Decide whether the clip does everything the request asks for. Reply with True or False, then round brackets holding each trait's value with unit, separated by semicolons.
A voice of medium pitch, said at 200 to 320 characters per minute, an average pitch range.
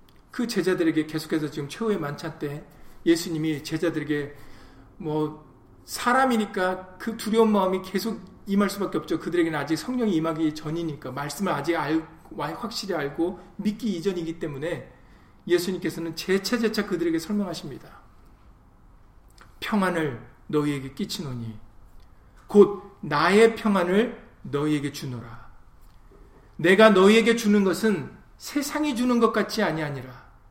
False (165 Hz; 300 characters per minute; 6.4 semitones)